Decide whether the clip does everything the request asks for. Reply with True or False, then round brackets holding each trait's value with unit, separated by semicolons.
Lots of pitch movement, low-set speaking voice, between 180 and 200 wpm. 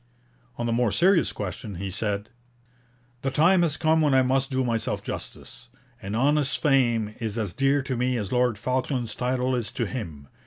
False (3.8 semitones; 125 Hz; 185 wpm)